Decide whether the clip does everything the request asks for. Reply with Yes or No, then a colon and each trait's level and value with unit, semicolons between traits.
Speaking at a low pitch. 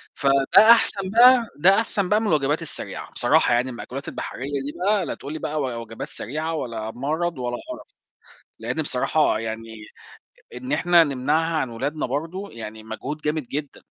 No: medium, 145 Hz